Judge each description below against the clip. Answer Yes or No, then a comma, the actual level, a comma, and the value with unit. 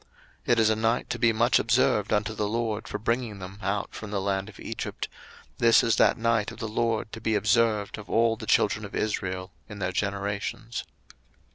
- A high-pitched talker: No, low, 110 Hz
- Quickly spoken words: Yes, fast, 210 wpm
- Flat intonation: Yes, narrow, 2.2 semitones